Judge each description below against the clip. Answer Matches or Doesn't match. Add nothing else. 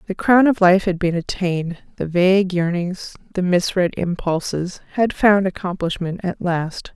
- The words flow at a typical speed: Matches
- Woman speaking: Matches